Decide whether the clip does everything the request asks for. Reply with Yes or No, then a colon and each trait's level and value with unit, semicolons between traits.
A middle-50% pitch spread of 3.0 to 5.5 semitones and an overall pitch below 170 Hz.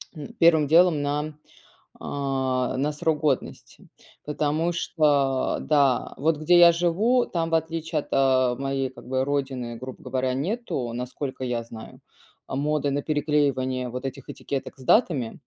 Yes: average, 3.3 semitones; medium, 140 Hz